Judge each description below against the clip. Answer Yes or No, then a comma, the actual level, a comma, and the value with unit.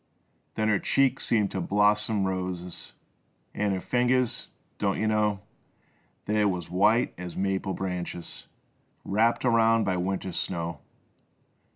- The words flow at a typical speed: No, slow, 130 wpm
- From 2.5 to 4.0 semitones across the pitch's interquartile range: Yes, average, 2.9 semitones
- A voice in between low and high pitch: No, low, 100 Hz